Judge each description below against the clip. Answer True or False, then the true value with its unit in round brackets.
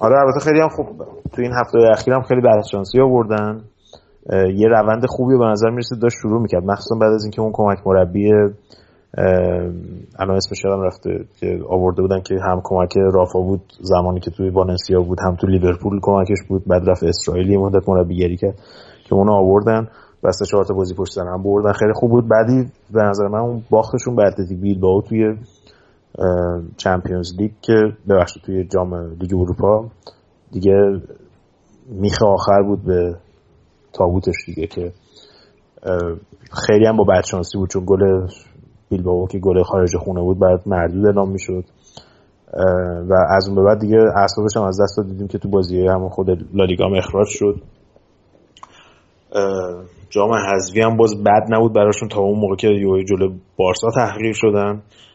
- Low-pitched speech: True (100 Hz)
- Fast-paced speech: True (165 wpm)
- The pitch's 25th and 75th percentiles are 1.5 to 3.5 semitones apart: True (2.7 semitones)